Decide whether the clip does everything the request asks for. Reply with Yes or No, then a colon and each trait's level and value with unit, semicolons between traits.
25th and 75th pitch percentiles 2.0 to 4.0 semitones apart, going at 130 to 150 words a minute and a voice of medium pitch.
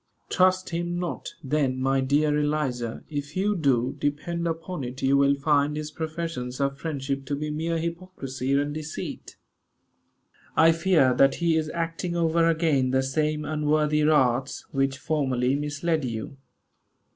Yes: average, 3.3 semitones; average, 145 wpm; medium, 150 Hz